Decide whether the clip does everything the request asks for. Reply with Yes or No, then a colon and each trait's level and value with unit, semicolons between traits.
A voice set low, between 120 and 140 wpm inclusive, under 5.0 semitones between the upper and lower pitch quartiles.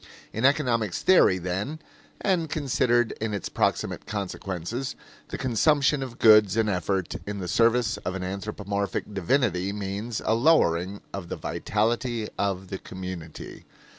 Yes: low, 105 Hz; slow, 135 wpm; average, 4.0 semitones